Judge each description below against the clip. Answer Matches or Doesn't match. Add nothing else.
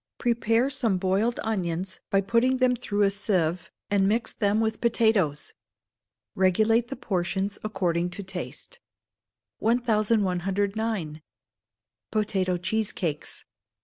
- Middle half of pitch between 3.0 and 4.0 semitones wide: Matches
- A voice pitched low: Doesn't match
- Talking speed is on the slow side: Matches